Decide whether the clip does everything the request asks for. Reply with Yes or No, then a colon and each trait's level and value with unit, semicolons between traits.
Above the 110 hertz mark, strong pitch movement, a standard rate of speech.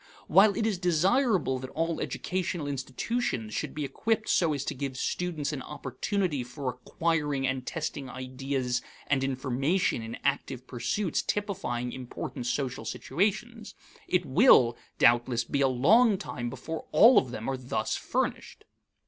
Yes: medium, 140 Hz; wide, 6.3 semitones; average, 145 wpm